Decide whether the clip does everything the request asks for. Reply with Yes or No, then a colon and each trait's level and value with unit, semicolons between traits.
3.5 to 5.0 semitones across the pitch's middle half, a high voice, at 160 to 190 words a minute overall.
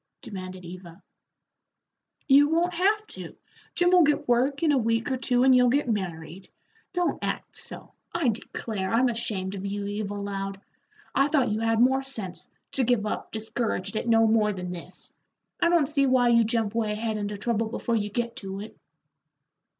Yes: average, 4.6 semitones; high, 225 Hz; average, 180 wpm